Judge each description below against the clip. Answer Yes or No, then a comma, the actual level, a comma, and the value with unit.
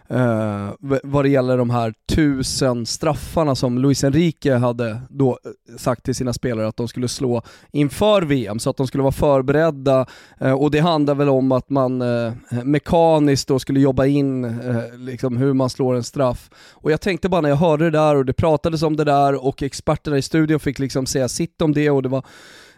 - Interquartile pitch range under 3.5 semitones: Yes, average, 2.9 semitones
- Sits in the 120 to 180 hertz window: Yes, low, 135 Hz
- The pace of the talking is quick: Yes, fast, 205 wpm